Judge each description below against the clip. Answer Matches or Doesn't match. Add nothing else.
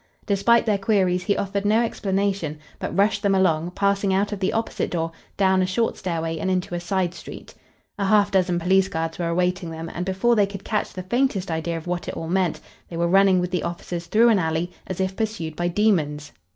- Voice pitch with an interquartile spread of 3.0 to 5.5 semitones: Doesn't match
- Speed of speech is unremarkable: Doesn't match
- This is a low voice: Doesn't match